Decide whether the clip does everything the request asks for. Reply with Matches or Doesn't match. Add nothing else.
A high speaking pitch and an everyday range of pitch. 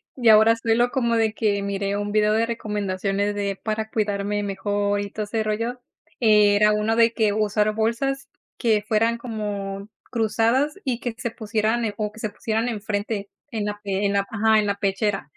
Doesn't match